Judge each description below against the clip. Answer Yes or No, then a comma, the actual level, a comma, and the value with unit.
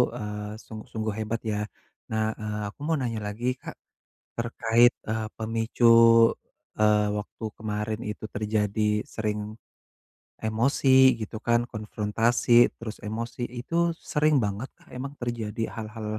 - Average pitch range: No, narrow, 1.9 semitones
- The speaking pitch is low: Yes, low, 110 Hz